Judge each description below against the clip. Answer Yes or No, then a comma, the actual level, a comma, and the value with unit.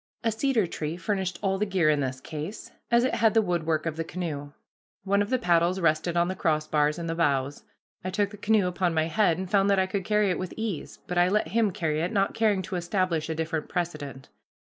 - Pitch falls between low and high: Yes, medium, 180 Hz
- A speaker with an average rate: No, fast, 235 wpm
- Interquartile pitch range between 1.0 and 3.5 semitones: No, average, 4.0 semitones